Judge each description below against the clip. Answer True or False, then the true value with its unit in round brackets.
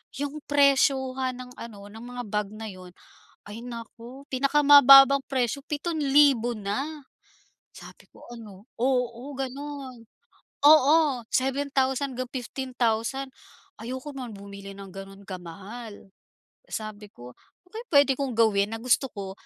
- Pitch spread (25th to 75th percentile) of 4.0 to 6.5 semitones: True (4.4 semitones)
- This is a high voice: True (250 Hz)